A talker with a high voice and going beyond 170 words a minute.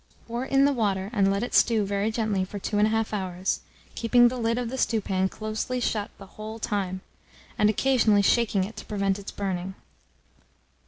Yes: high, 210 Hz; average, 180 wpm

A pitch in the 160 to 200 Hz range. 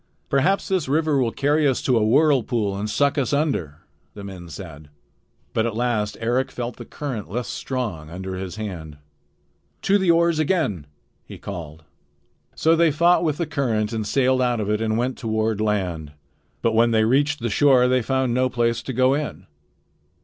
No: low, 120 Hz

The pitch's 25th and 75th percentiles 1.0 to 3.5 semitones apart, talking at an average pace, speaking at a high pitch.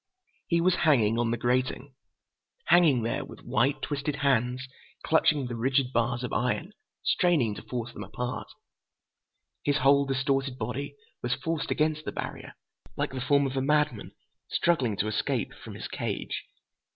No: average, 3.1 semitones; average, 155 wpm; low, 135 Hz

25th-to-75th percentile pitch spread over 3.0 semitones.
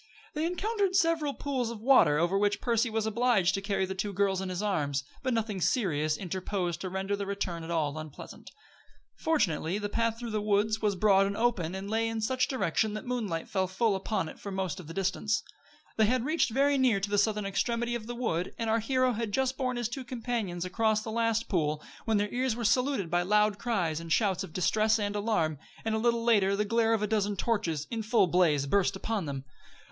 Yes: average, 3.7 semitones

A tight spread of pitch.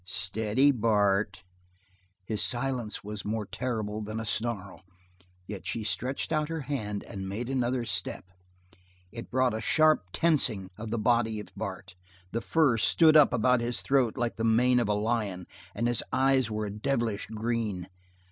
No: average, 3.2 semitones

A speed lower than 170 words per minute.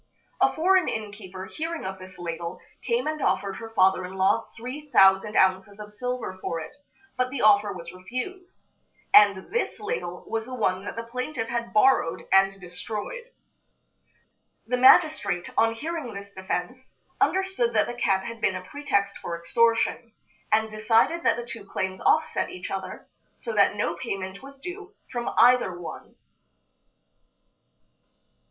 Yes: average, 155 wpm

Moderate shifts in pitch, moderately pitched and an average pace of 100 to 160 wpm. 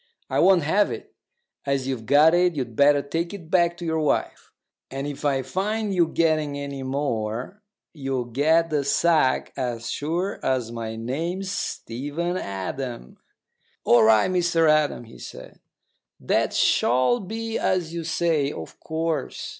Yes: average, 4.7 semitones; medium, 150 Hz; average, 150 wpm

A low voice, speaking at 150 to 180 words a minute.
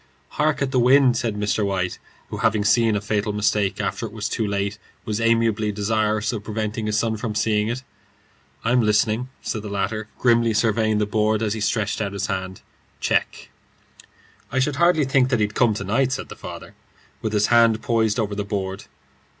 No: low, 110 Hz; average, 195 wpm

